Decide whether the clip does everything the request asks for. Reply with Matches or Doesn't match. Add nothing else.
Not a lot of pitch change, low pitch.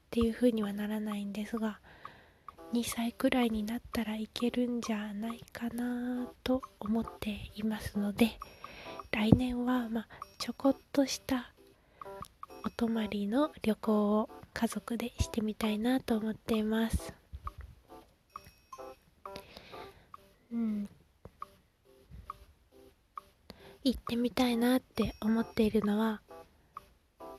Doesn't match